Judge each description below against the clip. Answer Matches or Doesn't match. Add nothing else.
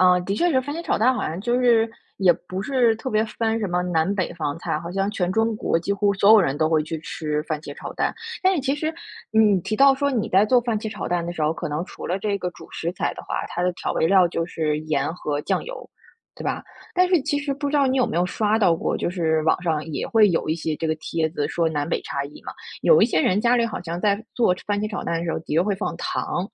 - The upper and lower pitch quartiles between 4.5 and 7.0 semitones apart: Matches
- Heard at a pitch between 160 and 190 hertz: Matches